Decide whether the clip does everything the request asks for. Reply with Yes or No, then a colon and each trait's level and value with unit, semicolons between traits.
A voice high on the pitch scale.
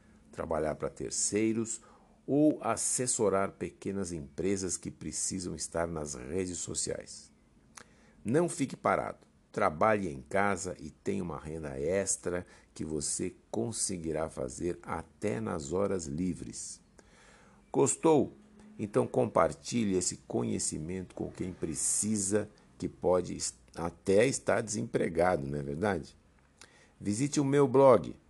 No: very low, 95 Hz